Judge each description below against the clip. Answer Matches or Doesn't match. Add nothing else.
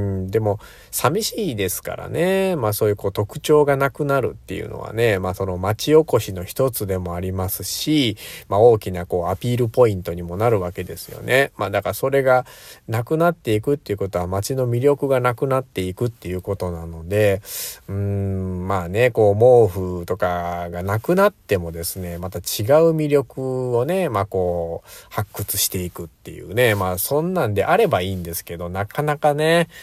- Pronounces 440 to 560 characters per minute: Doesn't match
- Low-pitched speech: Matches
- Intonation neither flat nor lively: Doesn't match